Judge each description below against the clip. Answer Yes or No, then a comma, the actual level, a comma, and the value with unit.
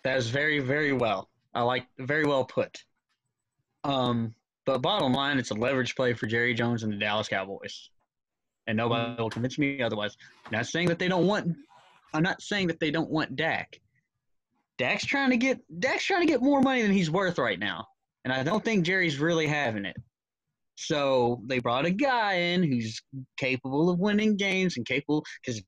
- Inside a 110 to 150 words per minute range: No, average, 190 wpm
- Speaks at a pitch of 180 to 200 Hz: No, medium, 140 Hz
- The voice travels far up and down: Yes, wide, 6.3 semitones